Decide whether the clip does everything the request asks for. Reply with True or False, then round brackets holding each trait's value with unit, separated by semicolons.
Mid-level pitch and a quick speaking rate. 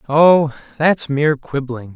False (145 Hz; 125 wpm)